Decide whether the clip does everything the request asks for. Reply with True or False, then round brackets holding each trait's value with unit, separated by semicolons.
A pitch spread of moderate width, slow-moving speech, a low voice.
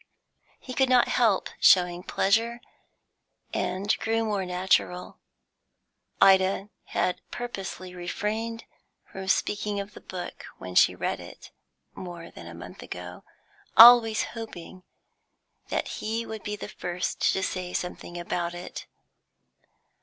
False (3.9 semitones; 125 wpm; 190 Hz)